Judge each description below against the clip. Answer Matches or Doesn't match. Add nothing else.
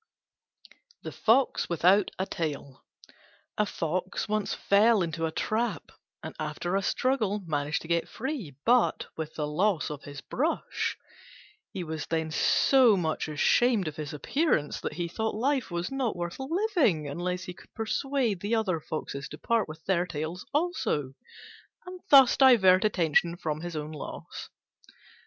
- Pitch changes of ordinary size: Doesn't match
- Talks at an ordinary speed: Matches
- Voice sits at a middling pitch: Matches